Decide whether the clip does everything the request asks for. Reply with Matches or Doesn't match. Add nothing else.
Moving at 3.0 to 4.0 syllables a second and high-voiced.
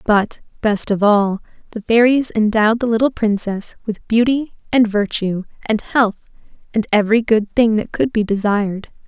Doesn't match